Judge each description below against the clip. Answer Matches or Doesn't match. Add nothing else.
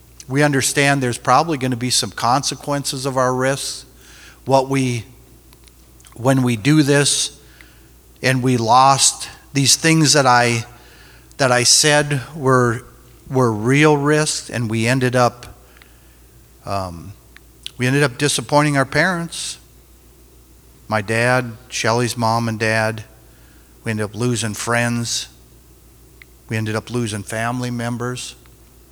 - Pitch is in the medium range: Doesn't match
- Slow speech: Matches